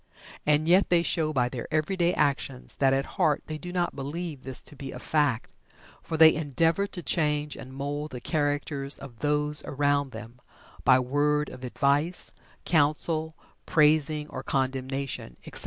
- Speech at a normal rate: Yes, average, 160 wpm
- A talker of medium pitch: Yes, medium, 145 Hz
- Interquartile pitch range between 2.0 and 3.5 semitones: Yes, narrow, 2.5 semitones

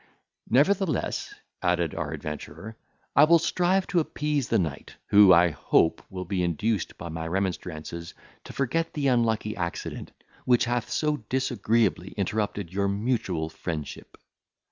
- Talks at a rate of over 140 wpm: No, slow, 135 wpm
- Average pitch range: No, wide, 7.3 semitones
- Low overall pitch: Yes, low, 100 Hz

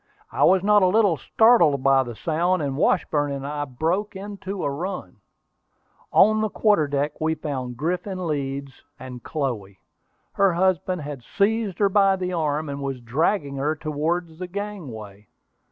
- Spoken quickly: No, average, 160 wpm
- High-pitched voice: No, medium, 155 Hz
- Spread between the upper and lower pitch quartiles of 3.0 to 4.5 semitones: No, wide, 5.4 semitones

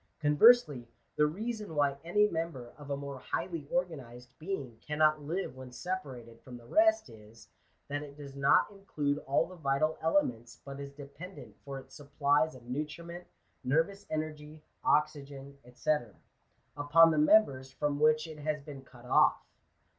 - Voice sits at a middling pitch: Yes, medium, 145 Hz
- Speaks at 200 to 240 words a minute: No, average, 155 wpm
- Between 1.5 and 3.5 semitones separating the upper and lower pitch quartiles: Yes, average, 3.0 semitones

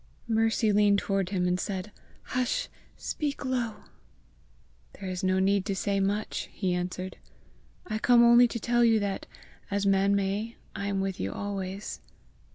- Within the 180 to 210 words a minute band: No, average, 160 wpm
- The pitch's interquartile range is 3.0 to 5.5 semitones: No, narrow, 2.6 semitones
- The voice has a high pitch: Yes, high, 200 Hz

